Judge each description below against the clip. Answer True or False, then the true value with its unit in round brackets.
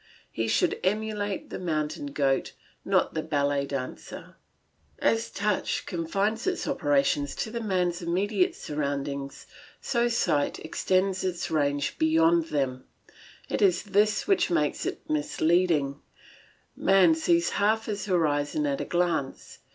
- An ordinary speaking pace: False (130 wpm)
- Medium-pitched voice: True (170 Hz)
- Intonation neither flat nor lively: False (5.8 semitones)